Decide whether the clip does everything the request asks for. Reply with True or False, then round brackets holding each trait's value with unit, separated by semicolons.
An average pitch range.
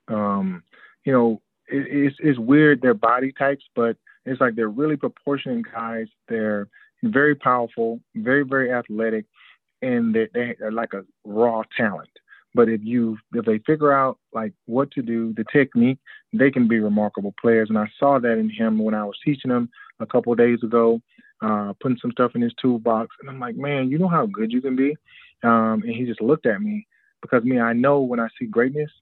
True (3.5 semitones)